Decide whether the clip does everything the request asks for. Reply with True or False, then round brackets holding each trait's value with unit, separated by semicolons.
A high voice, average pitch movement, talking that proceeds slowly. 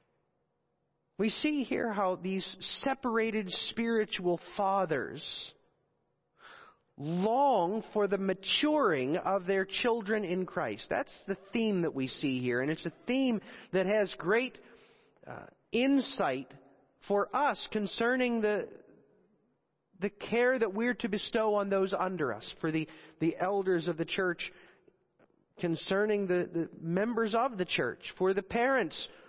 True (200 Hz; 4.3 semitones; 130 wpm)